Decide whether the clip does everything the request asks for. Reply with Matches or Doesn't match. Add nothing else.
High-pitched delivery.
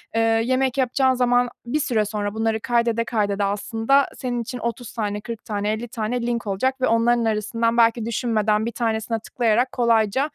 Matches